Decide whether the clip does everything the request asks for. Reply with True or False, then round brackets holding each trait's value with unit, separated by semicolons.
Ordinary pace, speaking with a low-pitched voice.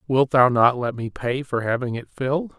False (230 wpm; 130 Hz)